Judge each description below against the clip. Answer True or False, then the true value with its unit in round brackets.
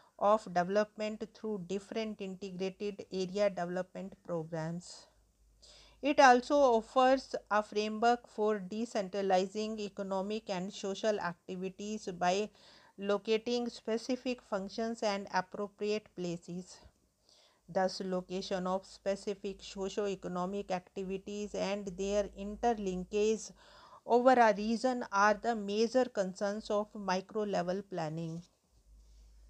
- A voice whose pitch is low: False (205 Hz)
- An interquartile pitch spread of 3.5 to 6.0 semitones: False (2.4 semitones)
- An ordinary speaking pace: False (95 wpm)